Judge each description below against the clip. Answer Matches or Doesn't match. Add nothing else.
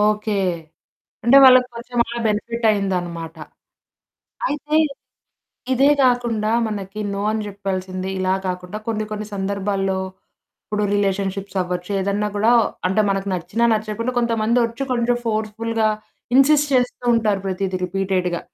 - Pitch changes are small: Doesn't match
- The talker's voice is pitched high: Matches